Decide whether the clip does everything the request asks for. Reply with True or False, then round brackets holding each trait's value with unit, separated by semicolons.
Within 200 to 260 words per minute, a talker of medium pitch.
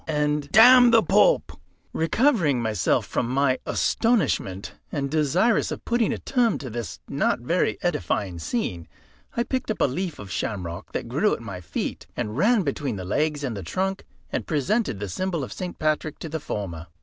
False (180 wpm; 150 Hz)